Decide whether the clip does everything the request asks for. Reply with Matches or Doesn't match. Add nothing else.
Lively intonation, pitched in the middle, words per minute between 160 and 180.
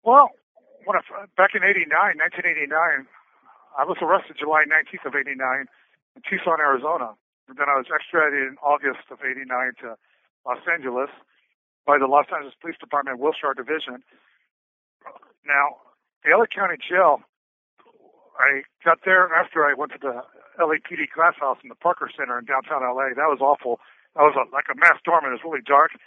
Doesn't match